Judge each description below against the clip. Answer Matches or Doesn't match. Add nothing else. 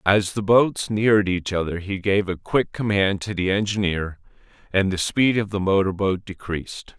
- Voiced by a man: Matches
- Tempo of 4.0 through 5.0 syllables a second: Matches